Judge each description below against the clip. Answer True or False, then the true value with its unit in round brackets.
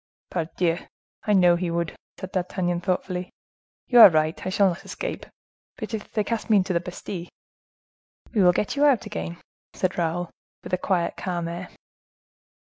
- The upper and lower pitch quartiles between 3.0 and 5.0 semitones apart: False (2.6 semitones)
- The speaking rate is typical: True (170 wpm)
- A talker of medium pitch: True (180 Hz)